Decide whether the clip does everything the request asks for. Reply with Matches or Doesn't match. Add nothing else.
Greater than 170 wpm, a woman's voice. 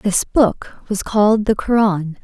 Doesn't match